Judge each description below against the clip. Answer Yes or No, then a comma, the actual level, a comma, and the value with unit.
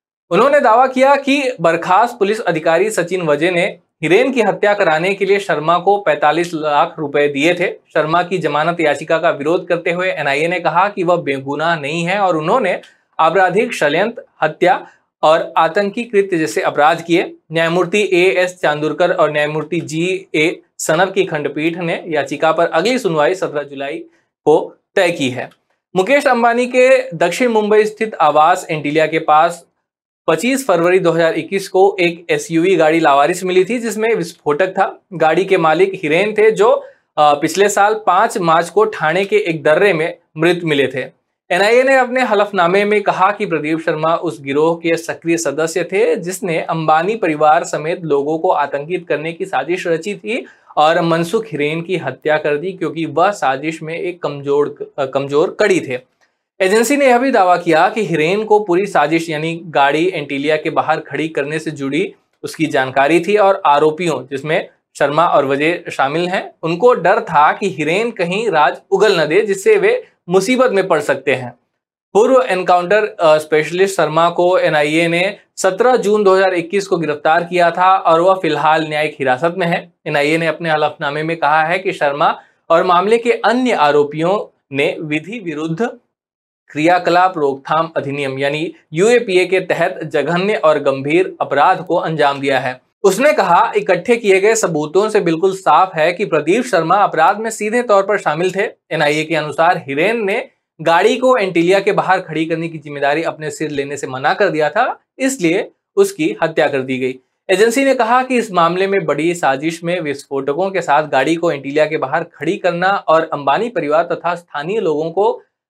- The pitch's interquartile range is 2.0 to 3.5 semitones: No, average, 4.3 semitones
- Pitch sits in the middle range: Yes, medium, 170 Hz